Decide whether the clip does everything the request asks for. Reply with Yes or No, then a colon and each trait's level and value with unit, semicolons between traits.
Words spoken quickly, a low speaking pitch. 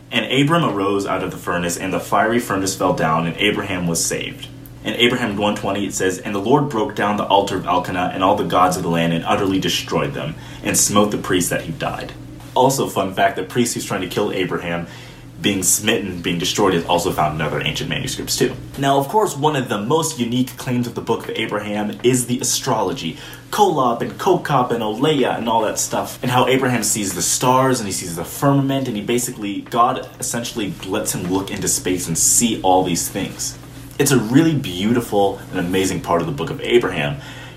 Yes: fast, 215 wpm; low, 110 Hz